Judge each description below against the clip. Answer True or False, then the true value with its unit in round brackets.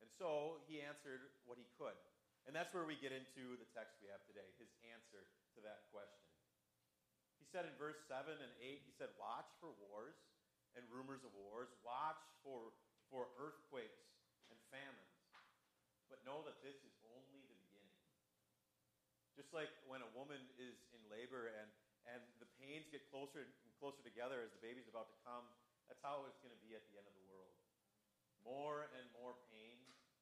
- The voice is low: True (125 Hz)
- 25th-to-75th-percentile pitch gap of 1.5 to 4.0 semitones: True (3.5 semitones)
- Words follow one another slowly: False (185 wpm)